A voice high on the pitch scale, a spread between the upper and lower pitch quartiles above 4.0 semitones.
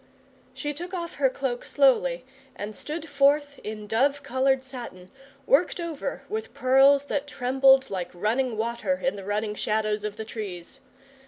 Yes: very high, 265 Hz; average, 4.7 semitones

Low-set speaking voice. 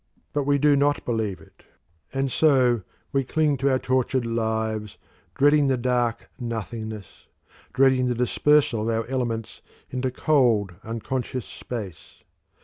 Yes: low, 125 Hz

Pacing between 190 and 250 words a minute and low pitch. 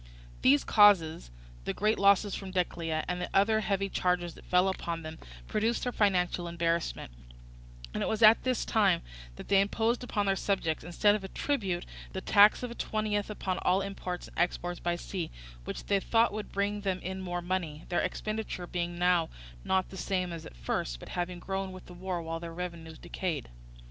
No: average, 195 wpm; medium, 185 Hz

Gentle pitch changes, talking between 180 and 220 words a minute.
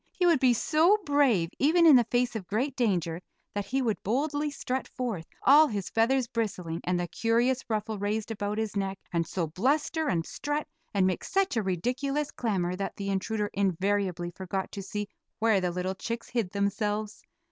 No: average, 5.2 semitones; average, 185 wpm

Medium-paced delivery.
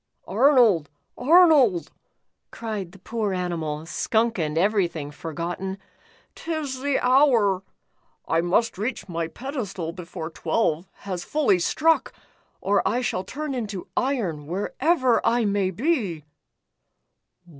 No: slow, 115 wpm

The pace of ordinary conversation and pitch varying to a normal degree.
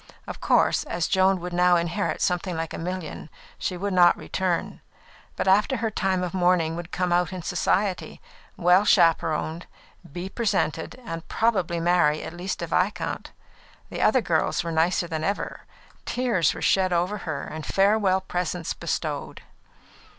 No: average, 160 wpm; narrow, 2.2 semitones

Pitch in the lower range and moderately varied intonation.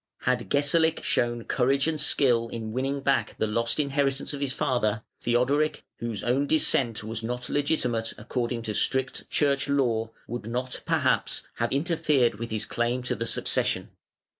Yes: low, 125 Hz; average, 3.2 semitones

